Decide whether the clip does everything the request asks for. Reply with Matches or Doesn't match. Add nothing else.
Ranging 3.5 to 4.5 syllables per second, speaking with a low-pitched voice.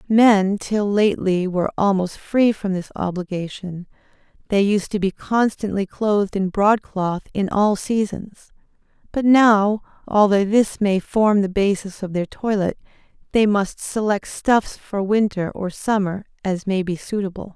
Doesn't match